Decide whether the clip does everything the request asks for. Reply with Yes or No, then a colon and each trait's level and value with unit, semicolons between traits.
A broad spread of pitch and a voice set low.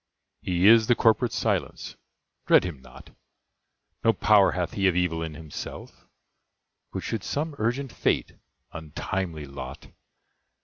Yes: wide, 5.7 semitones; very low, 90 Hz